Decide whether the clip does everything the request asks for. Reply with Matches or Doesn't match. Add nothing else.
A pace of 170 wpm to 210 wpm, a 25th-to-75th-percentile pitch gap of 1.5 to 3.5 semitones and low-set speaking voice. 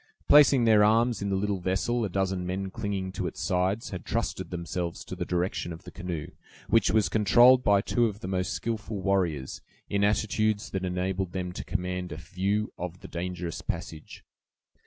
Matches